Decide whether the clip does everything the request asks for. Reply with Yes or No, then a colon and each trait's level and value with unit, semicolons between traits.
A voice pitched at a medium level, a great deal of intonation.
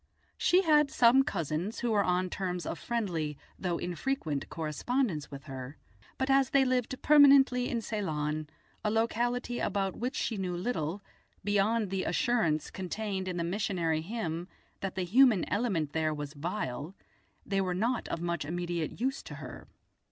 No: high, 195 Hz; wide, 6.5 semitones